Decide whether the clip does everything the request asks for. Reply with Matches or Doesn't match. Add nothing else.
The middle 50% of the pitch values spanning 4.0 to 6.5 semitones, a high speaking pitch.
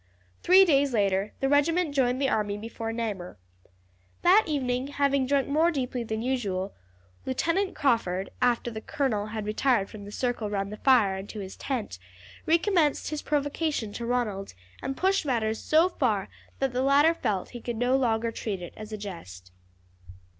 Matches